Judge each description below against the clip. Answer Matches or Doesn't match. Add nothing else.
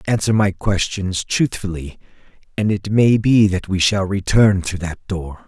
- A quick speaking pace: Doesn't match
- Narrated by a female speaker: Doesn't match